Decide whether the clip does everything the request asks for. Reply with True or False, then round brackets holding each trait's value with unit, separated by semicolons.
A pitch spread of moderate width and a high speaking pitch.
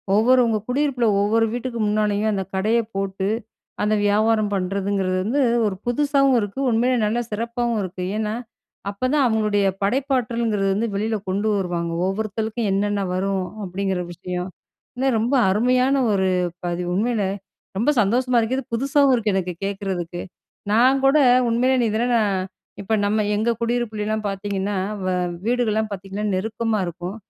True (3.4 semitones; 215 Hz)